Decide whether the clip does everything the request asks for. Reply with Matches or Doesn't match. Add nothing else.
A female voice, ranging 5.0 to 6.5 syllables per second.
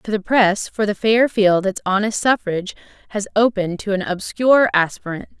Matches